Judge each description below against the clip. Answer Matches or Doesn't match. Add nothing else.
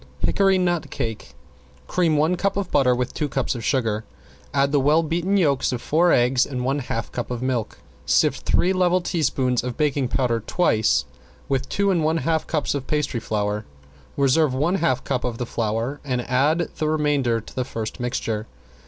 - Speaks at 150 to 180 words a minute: Doesn't match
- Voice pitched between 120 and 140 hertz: Matches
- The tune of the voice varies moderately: Matches